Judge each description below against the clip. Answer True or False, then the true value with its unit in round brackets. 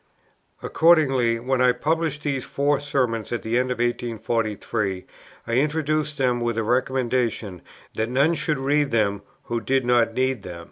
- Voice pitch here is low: True (125 Hz)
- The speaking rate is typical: True (155 wpm)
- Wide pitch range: False (3.6 semitones)